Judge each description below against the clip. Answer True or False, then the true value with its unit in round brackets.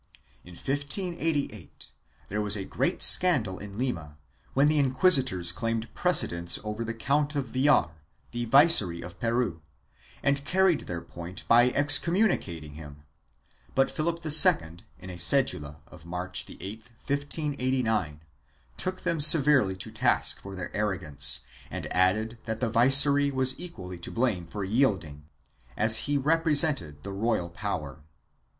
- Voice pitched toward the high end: False (115 Hz)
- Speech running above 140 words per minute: False (135 wpm)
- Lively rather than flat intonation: True (8.0 semitones)